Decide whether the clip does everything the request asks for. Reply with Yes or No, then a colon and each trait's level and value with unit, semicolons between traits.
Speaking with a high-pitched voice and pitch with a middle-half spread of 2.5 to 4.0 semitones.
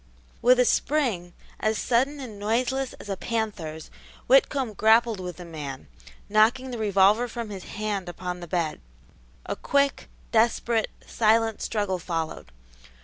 No: high, 215 Hz; average, 4.7 semitones